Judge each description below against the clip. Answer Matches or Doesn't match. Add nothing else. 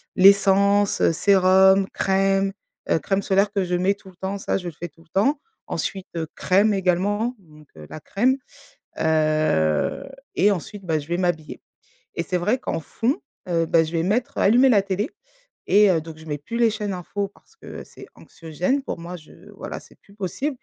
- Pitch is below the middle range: Doesn't match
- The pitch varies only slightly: Doesn't match